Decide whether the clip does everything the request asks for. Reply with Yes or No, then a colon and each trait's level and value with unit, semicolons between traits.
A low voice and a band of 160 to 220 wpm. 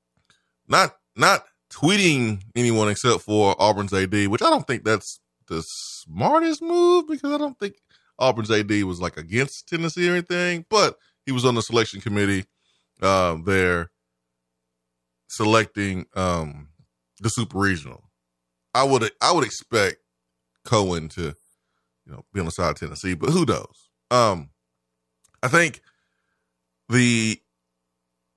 No: very low, 95 Hz; slow, 135 wpm